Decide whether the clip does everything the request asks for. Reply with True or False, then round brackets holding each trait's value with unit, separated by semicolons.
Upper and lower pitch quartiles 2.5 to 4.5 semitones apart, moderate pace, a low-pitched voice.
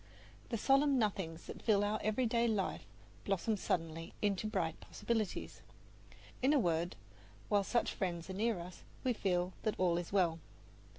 False (4.2 semitones; 155 wpm; 200 Hz)